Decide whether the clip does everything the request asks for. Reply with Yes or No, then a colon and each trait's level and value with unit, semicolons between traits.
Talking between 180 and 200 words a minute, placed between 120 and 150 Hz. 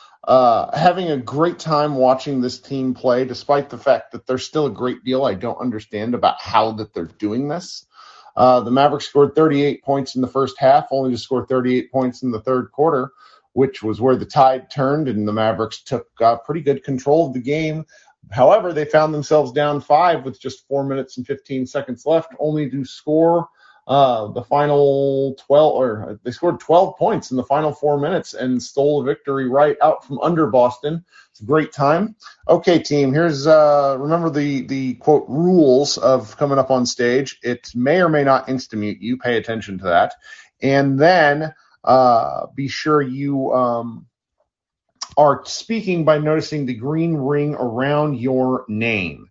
Yes: average, 185 wpm; medium, 140 Hz